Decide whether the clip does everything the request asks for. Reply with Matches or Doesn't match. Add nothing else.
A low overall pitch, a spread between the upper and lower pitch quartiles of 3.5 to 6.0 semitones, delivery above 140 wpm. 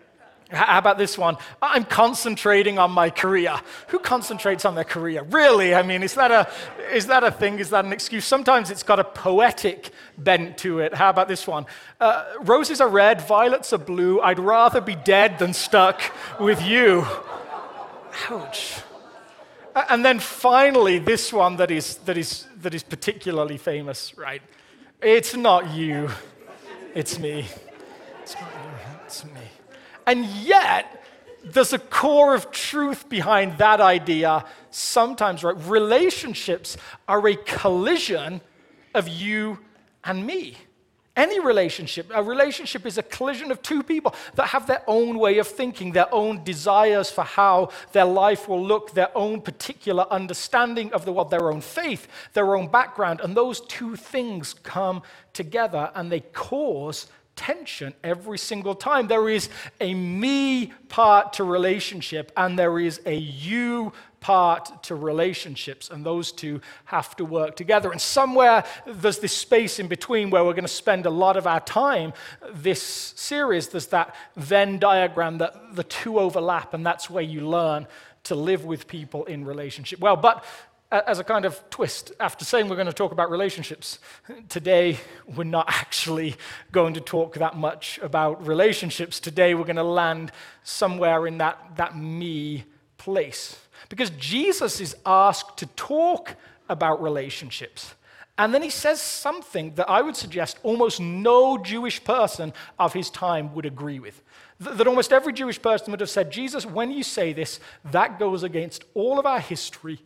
Doesn't match